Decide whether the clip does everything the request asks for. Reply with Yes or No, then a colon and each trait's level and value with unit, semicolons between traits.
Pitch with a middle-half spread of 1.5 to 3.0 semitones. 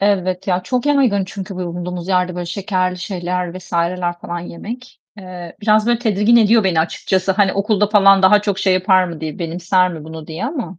Yes: narrow, 2.6 semitones